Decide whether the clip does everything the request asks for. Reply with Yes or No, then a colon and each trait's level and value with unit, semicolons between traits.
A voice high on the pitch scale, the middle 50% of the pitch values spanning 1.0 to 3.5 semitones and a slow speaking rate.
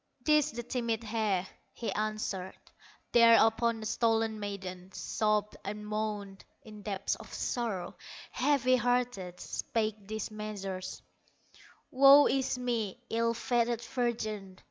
Yes: high, 220 Hz; narrow, 2.6 semitones; slow, 115 wpm